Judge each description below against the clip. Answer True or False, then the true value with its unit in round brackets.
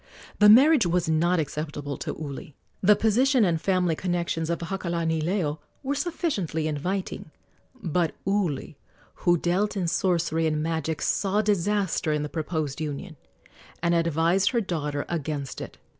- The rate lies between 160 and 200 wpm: False (140 wpm)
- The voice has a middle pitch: True (170 Hz)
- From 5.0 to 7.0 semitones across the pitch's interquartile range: False (3.8 semitones)